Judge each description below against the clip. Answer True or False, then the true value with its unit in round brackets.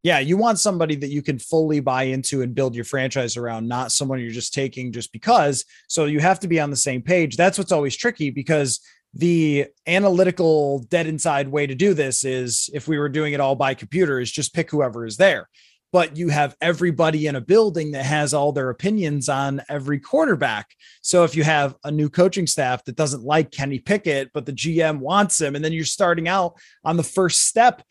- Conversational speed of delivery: False (215 wpm)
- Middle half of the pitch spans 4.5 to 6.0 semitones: False (3.8 semitones)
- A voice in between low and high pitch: True (150 Hz)